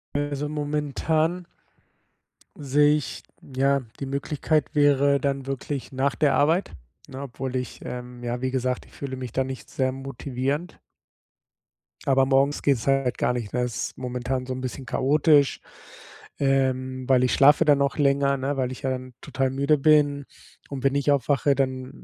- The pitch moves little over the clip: Yes, narrow, 1.8 semitones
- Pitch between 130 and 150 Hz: Yes, low, 135 Hz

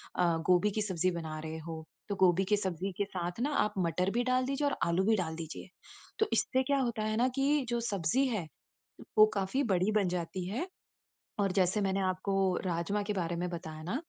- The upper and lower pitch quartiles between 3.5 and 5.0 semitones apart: Yes, average, 4.4 semitones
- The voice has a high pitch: Yes, high, 195 Hz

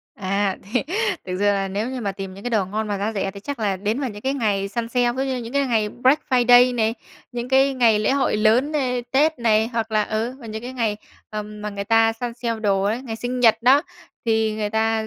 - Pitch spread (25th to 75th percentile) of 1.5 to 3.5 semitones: Yes, average, 2.9 semitones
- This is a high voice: Yes, high, 225 Hz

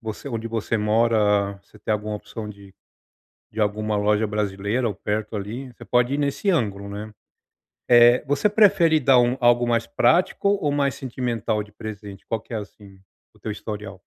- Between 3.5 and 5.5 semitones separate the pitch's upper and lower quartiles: No, average, 3.0 semitones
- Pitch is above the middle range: No, low, 110 Hz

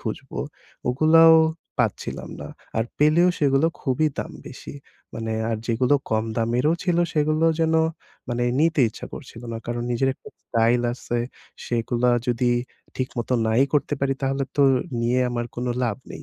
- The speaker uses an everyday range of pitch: Yes, average, 4.0 semitones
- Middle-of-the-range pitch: No, low, 125 Hz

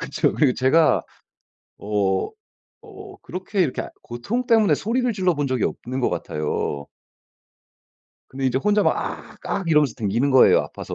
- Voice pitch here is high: No, medium, 145 Hz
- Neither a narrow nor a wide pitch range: No, wide, 9.0 semitones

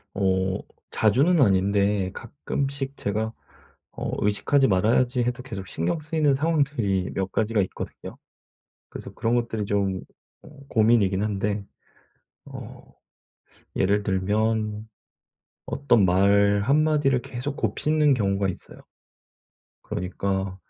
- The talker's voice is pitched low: Yes, low, 105 Hz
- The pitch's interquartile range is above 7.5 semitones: No, average, 5.2 semitones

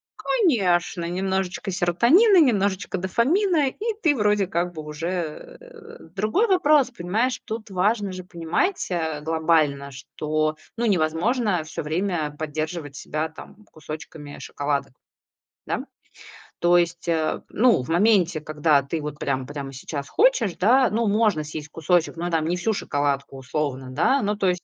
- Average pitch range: No, wide, 5.8 semitones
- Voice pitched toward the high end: No, medium, 175 Hz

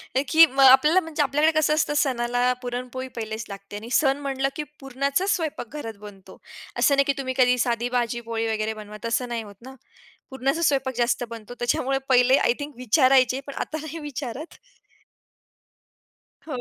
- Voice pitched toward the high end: Yes, very high, 260 Hz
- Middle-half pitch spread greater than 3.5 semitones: No, average, 2.9 semitones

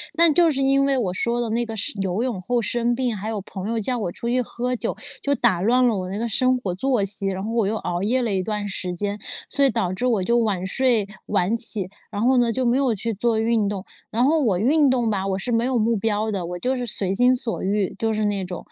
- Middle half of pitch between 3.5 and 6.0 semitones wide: Yes, average, 3.9 semitones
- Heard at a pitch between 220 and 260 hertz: Yes, high, 225 Hz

